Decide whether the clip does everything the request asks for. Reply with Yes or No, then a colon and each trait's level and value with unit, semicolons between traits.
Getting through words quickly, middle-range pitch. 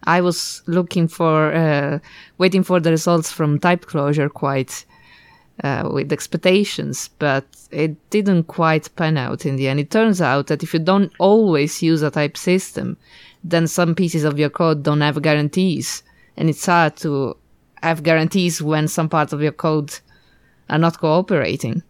No: average, 165 wpm; medium, 160 Hz